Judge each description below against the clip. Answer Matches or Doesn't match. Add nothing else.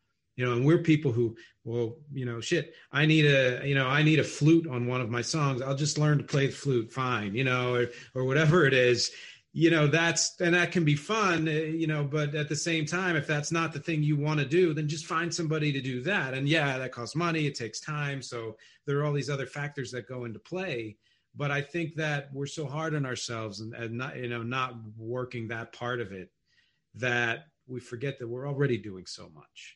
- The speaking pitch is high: Doesn't match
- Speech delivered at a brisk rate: Matches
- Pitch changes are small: Doesn't match